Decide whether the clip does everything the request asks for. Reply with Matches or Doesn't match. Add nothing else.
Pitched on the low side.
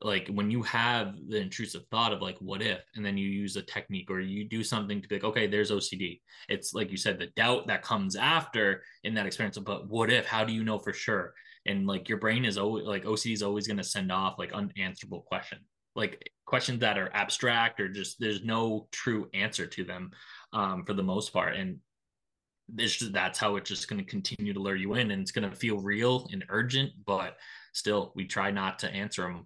Matches